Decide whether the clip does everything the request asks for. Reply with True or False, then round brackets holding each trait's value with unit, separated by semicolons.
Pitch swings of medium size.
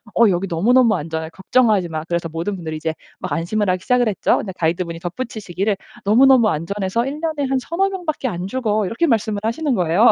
False (6.4 semitones)